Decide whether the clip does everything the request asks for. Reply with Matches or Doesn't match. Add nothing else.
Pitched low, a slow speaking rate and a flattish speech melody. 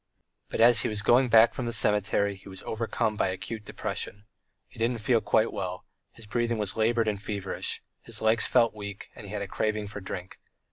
Doesn't match